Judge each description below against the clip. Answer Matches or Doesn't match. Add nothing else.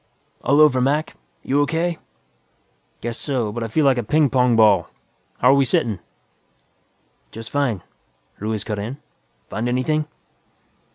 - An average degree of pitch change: Matches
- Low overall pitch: Matches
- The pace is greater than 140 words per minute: Doesn't match